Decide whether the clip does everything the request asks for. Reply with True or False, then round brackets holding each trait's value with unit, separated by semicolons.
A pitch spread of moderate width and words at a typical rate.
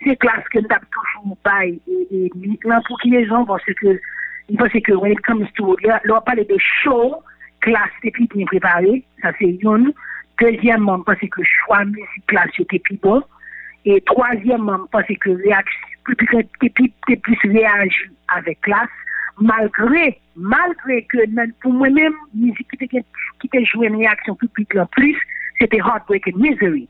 True (3.9 semitones; 155 wpm)